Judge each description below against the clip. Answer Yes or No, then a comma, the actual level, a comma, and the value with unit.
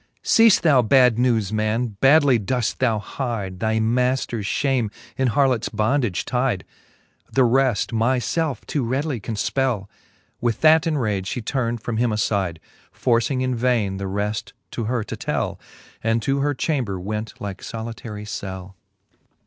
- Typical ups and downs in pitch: Yes, average, 3.6 semitones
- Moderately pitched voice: No, low, 115 Hz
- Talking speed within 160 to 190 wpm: No, average, 150 wpm